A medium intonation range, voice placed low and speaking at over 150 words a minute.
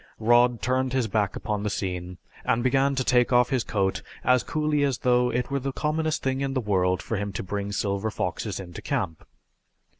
Yes: average, 4.6 semitones; low, 120 Hz; fast, 205 wpm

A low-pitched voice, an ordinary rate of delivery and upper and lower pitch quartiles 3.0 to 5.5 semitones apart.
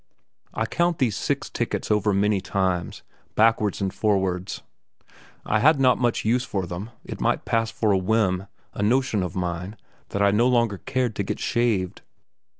Yes: low, 105 Hz; average, 170 wpm; average, 3.6 semitones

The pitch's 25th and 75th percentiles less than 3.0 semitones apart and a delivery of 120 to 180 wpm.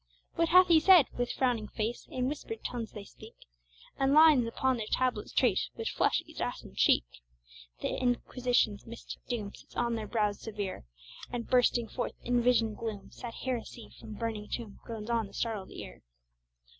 Yes: narrow, 2.6 semitones; average, 170 wpm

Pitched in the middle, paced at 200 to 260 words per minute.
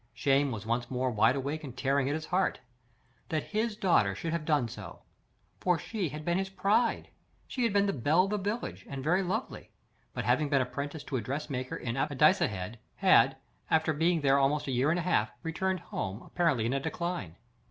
Yes: medium, 150 Hz; fast, 205 wpm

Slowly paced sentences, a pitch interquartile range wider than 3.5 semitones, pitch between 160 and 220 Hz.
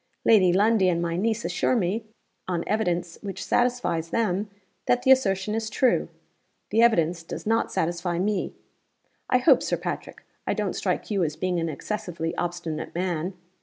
No: average, 165 wpm; average, 4.3 semitones; medium, 185 Hz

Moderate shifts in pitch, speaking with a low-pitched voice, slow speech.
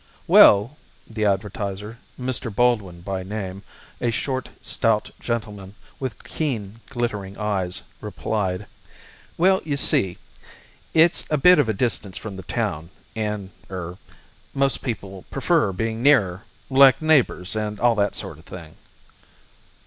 Yes: average, 4.2 semitones; low, 105 Hz; slow, 130 wpm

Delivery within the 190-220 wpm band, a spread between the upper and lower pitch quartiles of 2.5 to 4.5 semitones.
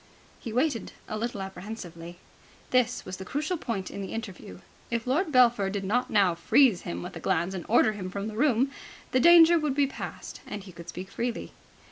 No: average, 200 wpm; average, 5.1 semitones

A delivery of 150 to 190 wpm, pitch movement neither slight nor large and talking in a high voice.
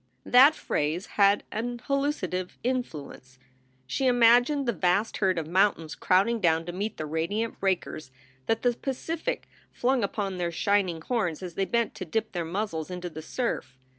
No: average, 165 wpm; wide, 5.7 semitones; high, 200 Hz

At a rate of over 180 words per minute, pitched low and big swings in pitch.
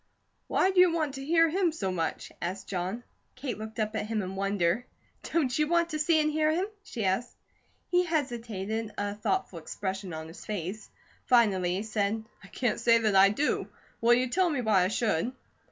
No: average, 200 wpm; high, 225 Hz; wide, 7.3 semitones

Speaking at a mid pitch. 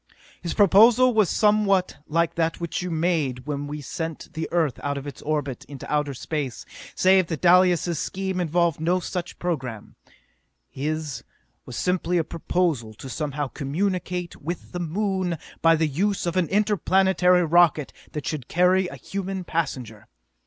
Yes: medium, 170 Hz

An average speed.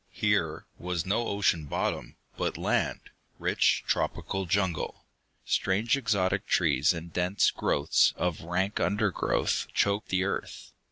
No: slow, 120 wpm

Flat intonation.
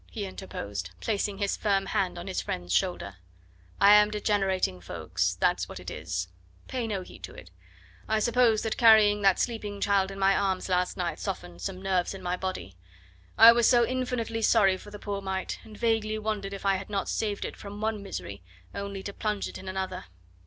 Yes: narrow, 2.3 semitones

